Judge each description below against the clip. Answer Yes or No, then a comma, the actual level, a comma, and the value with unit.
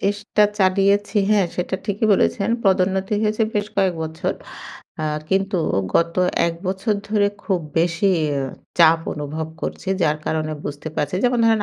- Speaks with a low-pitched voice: No, high, 190 Hz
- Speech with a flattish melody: No, average, 3.7 semitones